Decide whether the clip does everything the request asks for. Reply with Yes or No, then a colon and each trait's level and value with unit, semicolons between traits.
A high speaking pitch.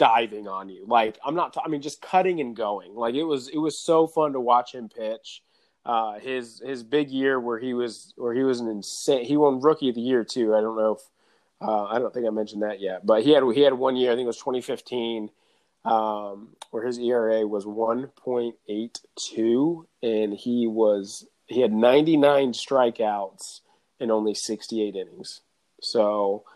No: low, 120 Hz